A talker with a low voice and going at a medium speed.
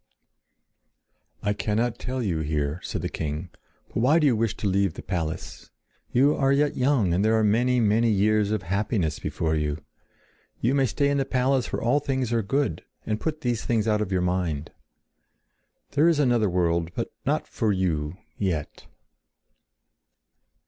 Yes: low, 105 Hz; average, 165 wpm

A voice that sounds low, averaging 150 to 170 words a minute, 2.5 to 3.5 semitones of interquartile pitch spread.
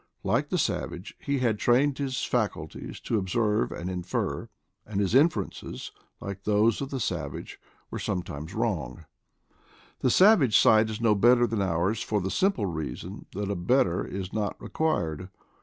No: low, 105 Hz; average, 160 wpm; average, 4.8 semitones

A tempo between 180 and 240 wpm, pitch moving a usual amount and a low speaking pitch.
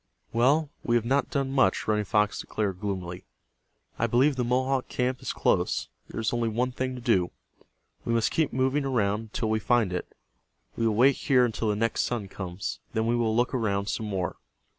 Yes: average, 200 wpm; average, 3.4 semitones; low, 115 Hz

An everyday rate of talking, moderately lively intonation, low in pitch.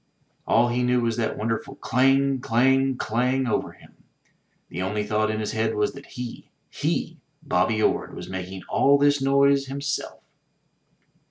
Yes: average, 155 wpm; average, 3.9 semitones; low, 125 Hz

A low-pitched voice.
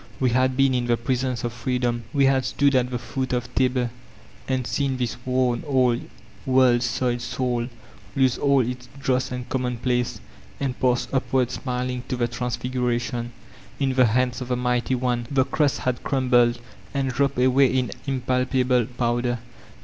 Yes: low, 125 Hz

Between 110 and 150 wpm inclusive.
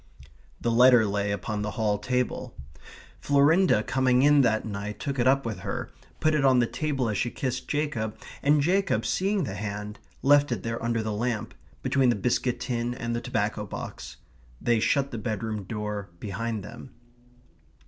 No: average, 175 wpm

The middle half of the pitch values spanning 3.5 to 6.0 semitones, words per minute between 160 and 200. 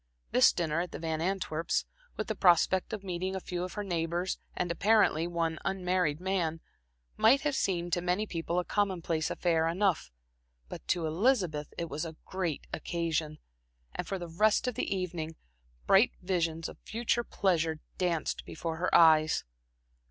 No: average, 2.7 semitones; average, 165 wpm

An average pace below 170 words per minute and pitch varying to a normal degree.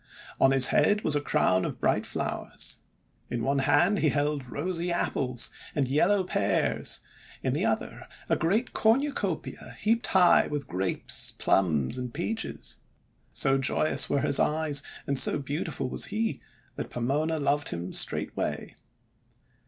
Yes: average, 145 wpm; average, 5.0 semitones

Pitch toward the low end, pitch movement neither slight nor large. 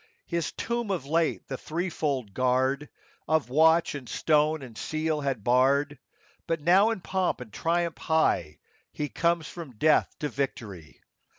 No: medium, 150 Hz; average, 4.2 semitones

